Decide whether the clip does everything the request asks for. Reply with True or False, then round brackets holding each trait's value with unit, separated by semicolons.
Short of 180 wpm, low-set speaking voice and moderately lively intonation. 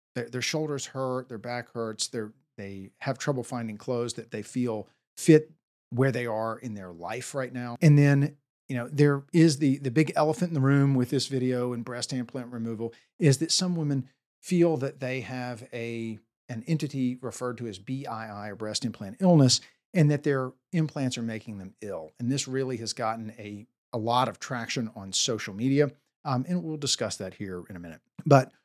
False (200 wpm; 125 Hz; 3.7 semitones)